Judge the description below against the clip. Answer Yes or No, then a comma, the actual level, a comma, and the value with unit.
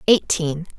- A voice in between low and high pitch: Yes, medium, 170 Hz